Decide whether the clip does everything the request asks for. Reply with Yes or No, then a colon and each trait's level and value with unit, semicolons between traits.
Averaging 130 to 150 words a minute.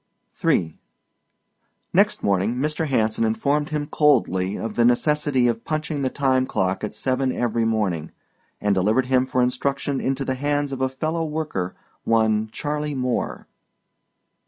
Yes: average, 145 wpm